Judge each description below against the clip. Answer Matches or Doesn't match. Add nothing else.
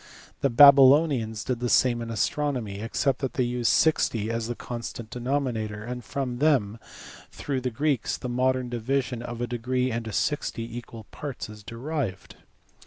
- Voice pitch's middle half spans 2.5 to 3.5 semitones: Matches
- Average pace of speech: Matches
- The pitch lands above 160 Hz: Doesn't match